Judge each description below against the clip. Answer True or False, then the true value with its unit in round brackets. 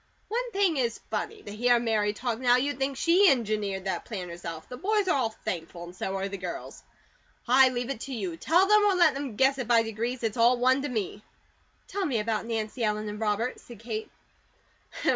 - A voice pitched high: True (235 Hz)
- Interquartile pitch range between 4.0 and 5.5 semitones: True (4.5 semitones)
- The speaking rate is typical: False (215 wpm)